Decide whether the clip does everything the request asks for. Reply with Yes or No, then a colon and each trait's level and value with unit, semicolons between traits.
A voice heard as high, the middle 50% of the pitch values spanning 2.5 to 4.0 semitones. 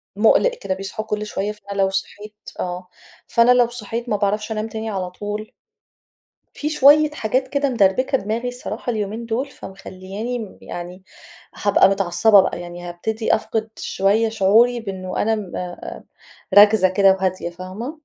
Yes: high, 210 Hz; average, 3.4 semitones